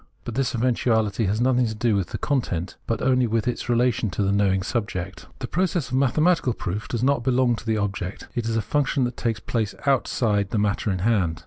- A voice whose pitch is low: Yes, low, 115 Hz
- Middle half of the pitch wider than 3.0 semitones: Yes, average, 3.7 semitones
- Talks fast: Yes, fast, 220 wpm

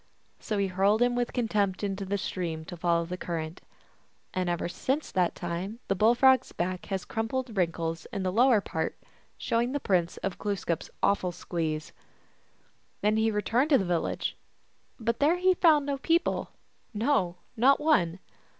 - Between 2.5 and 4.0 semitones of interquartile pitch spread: No, wide, 5.5 semitones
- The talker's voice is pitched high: Yes, high, 200 Hz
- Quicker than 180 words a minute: No, average, 175 wpm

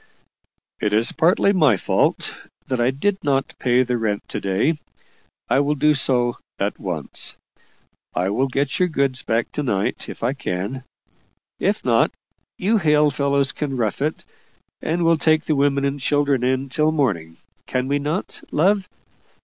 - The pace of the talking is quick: No, average, 165 wpm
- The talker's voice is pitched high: No, medium, 140 Hz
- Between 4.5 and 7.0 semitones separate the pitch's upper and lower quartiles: No, average, 3.8 semitones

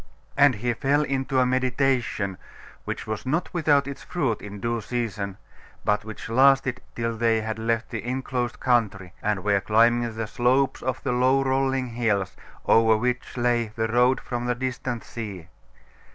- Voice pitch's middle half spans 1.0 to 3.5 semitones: Yes, average, 2.9 semitones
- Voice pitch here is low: Yes, low, 120 Hz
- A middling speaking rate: Yes, average, 165 wpm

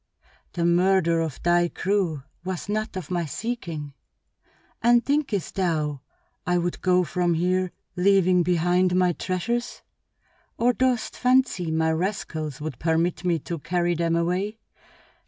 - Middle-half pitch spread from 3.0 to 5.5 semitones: No, narrow, 2.6 semitones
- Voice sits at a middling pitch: Yes, medium, 180 Hz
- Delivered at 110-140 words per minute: Yes, slow, 135 wpm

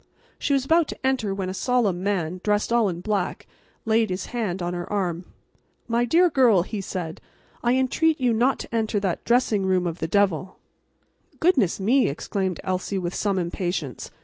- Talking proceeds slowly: No, average, 180 wpm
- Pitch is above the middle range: Yes, high, 200 Hz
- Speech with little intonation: No, average, 4.8 semitones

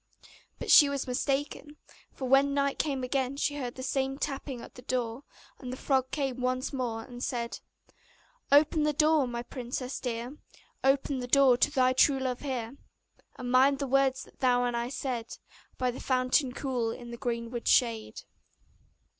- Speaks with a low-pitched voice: No, very high, 260 Hz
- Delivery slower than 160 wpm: No, average, 175 wpm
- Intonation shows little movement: Yes, narrow, 2.0 semitones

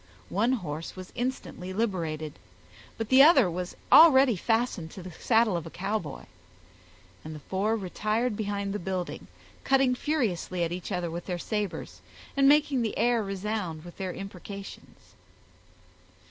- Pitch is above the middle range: Yes, high, 200 Hz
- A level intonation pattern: No, average, 4.9 semitones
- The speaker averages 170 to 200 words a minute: No, average, 145 wpm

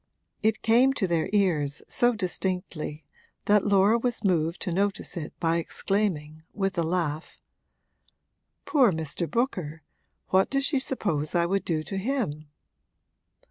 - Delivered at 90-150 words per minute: Yes, average, 140 wpm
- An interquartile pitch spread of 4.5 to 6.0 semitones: Yes, average, 5.0 semitones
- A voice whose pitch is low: No, medium, 185 Hz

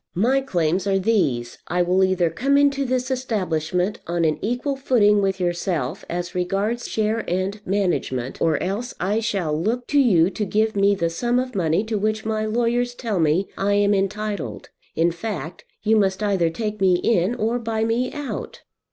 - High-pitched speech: Yes, high, 205 Hz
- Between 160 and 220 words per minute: Yes, average, 180 wpm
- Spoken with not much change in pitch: No, average, 4.3 semitones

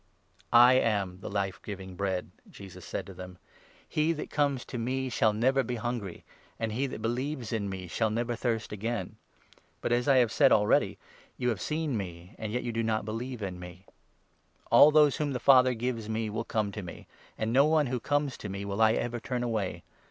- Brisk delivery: Yes, fast, 220 wpm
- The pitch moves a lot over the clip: No, average, 3.9 semitones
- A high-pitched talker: No, low, 115 Hz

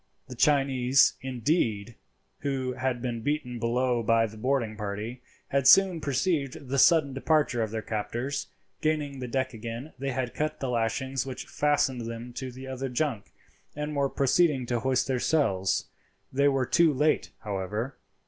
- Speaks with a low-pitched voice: Yes, low, 130 Hz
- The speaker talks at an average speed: Yes, average, 160 wpm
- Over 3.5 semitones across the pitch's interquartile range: No, average, 3.1 semitones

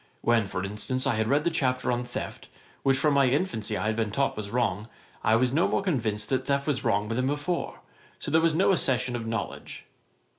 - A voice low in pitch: Yes, low, 125 Hz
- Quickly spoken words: Yes, fast, 220 wpm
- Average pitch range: Yes, average, 4.3 semitones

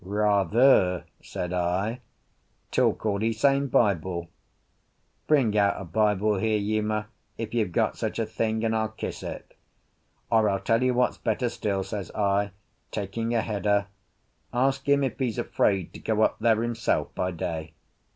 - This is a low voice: Yes, low, 110 Hz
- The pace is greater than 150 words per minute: Yes, average, 160 wpm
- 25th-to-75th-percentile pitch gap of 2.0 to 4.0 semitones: Yes, narrow, 2.6 semitones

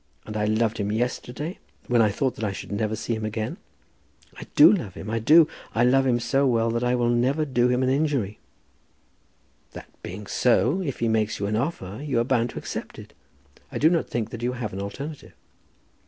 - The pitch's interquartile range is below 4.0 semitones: Yes, average, 3.6 semitones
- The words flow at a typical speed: No, fast, 215 wpm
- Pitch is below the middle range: Yes, low, 120 Hz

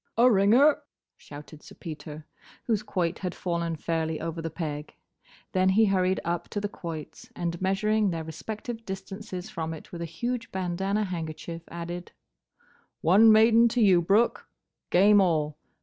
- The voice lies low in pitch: No, medium, 185 Hz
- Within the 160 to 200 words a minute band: No, average, 150 wpm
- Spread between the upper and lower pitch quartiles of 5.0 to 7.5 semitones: No, average, 4.1 semitones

